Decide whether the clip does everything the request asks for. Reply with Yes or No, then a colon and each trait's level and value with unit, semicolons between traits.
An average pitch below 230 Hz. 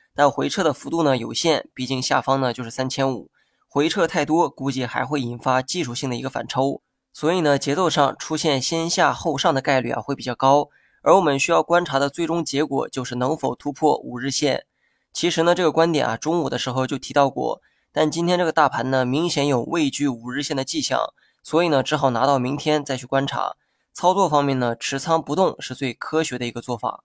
Yes: medium, 140 Hz